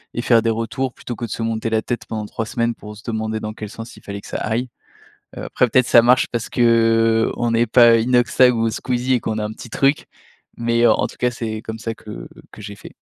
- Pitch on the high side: No, low, 115 Hz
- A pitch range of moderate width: No, narrow, 1.5 semitones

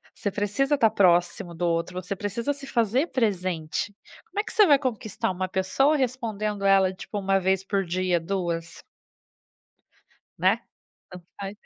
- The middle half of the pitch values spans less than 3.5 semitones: No, average, 4.0 semitones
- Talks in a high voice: Yes, high, 195 Hz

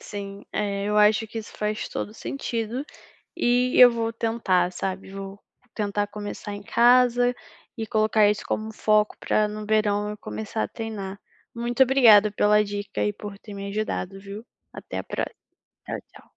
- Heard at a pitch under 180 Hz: No, high, 210 Hz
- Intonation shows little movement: Yes, narrow, 1.9 semitones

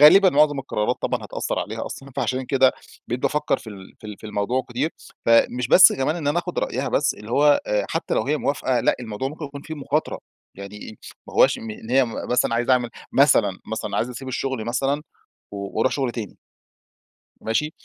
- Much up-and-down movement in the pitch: No, average, 4.2 semitones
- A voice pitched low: Yes, low, 130 Hz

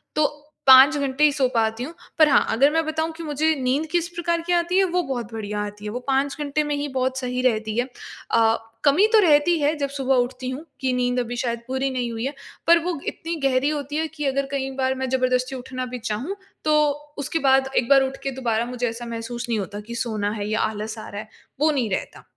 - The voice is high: Yes, very high, 265 Hz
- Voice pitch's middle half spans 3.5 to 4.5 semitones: Yes, average, 3.9 semitones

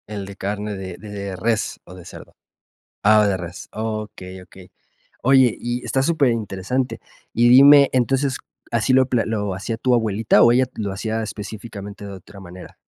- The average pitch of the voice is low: Yes, low, 110 Hz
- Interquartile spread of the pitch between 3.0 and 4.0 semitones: Yes, average, 3.6 semitones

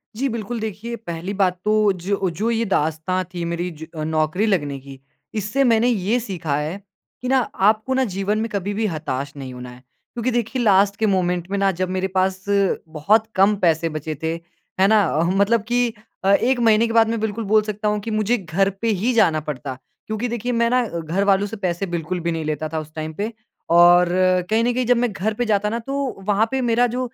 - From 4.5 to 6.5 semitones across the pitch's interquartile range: Yes, average, 4.8 semitones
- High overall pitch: Yes, high, 200 Hz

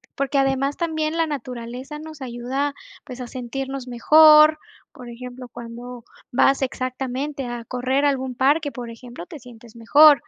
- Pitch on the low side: No, very high, 260 Hz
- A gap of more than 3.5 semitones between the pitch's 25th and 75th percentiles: No, average, 2.8 semitones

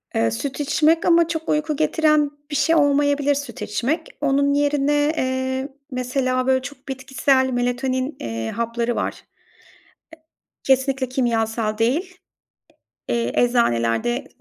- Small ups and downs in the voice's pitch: No, average, 3.1 semitones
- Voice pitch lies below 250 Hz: No, very high, 265 Hz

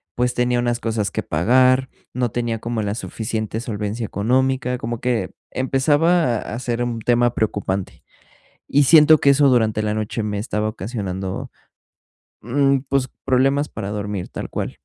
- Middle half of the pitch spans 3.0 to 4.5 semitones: Yes, average, 3.4 semitones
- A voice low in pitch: Yes, low, 120 Hz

